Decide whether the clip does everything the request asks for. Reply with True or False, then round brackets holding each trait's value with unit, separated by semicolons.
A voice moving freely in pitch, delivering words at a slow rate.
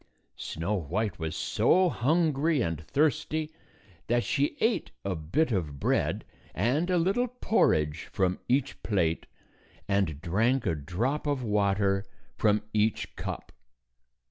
True (8.8 semitones; 125 wpm)